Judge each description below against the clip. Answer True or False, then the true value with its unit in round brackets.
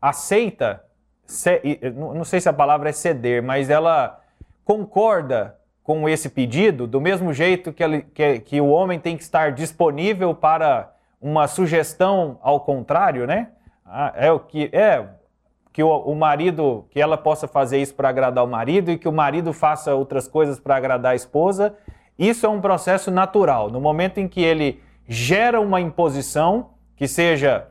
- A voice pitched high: False (155 Hz)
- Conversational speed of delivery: True (160 wpm)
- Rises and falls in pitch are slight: False (4.2 semitones)